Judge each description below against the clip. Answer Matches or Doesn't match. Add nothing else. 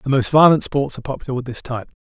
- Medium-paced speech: Doesn't match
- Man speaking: Matches